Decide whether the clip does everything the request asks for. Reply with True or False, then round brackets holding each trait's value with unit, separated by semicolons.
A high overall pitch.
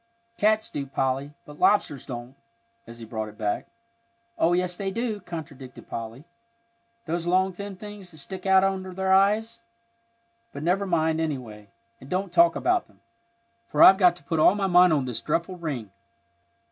False (175 Hz)